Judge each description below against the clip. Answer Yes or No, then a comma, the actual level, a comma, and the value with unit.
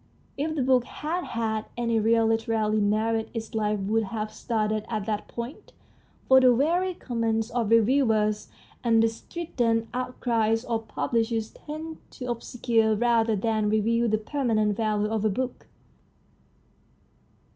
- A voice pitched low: No, high, 225 Hz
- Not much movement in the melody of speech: Yes, narrow, 2.0 semitones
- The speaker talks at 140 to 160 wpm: Yes, average, 145 wpm